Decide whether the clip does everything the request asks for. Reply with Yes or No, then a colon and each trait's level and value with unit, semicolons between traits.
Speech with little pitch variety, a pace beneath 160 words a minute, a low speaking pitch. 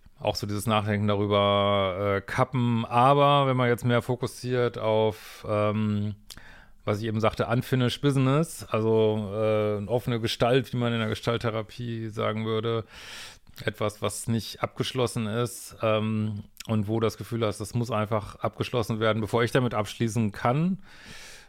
Yes: narrow, 2.2 semitones; average, 150 wpm; low, 110 Hz